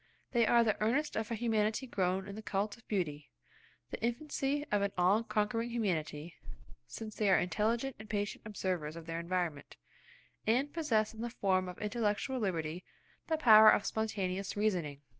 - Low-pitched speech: No, high, 210 Hz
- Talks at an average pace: Yes, average, 165 wpm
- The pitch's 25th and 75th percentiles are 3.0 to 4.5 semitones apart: Yes, average, 3.9 semitones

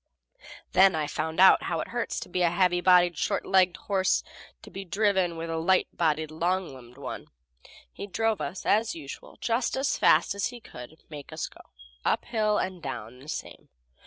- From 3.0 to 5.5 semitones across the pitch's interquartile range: Yes, average, 3.9 semitones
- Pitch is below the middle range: No, medium, 180 Hz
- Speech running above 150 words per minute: Yes, average, 175 wpm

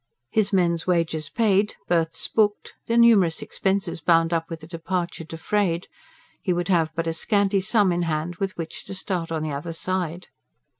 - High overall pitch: No, medium, 175 Hz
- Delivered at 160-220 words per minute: Yes, average, 180 wpm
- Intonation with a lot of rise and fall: No, average, 3.0 semitones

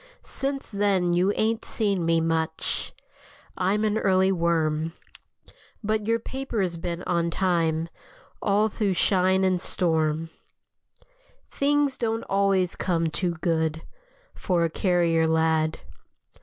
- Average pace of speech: No, slow, 115 wpm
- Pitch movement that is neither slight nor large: Yes, average, 3.8 semitones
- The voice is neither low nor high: Yes, medium, 180 Hz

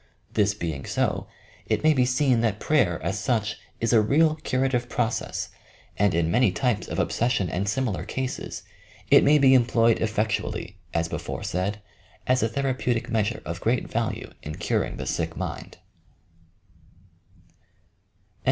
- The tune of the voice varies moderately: Yes, average, 4.1 semitones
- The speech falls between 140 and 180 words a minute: Yes, average, 145 wpm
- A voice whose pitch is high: No, low, 115 Hz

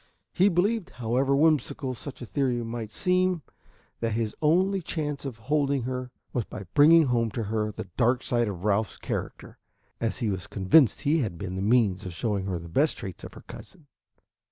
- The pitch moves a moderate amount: No, wide, 5.8 semitones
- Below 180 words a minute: No, average, 190 wpm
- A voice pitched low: Yes, low, 125 Hz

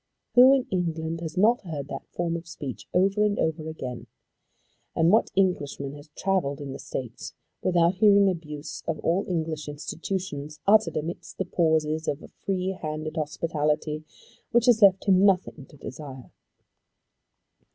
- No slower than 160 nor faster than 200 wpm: No, average, 150 wpm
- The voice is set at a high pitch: No, medium, 165 Hz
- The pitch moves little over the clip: No, average, 4.0 semitones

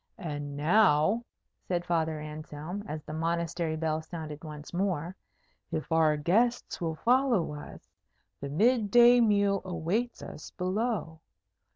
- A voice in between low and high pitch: Yes, medium, 170 Hz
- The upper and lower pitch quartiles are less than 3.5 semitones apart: No, average, 4.8 semitones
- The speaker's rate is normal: No, slow, 130 wpm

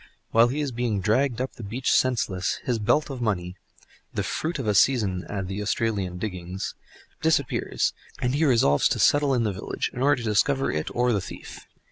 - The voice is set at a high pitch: No, low, 115 Hz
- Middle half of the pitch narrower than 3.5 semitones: No, average, 5.1 semitones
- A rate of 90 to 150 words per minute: No, average, 185 wpm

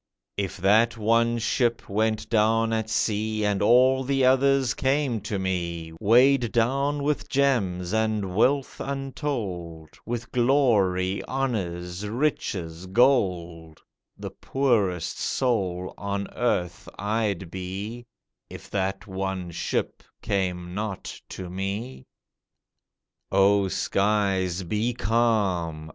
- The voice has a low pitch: Yes, low, 105 Hz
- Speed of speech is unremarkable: No, slow, 105 wpm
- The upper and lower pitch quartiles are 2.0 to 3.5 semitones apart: No, average, 4.5 semitones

